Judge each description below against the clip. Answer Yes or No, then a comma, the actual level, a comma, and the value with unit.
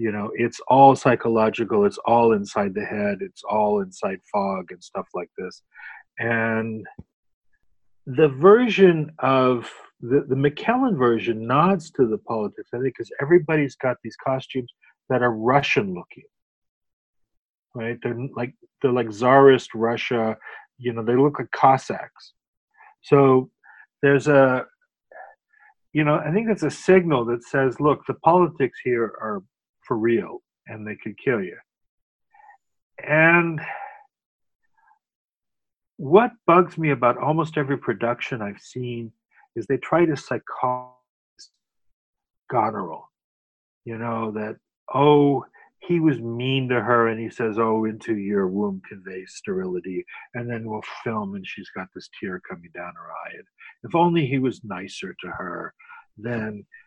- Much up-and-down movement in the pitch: Yes, wide, 5.8 semitones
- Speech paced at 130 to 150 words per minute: Yes, average, 140 wpm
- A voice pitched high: No, low, 130 Hz